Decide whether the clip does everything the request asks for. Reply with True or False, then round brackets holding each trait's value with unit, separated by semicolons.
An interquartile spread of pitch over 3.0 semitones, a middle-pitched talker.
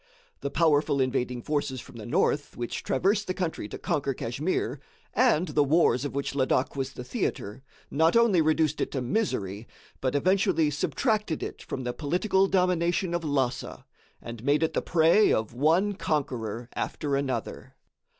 True (5.2 semitones; 145 Hz)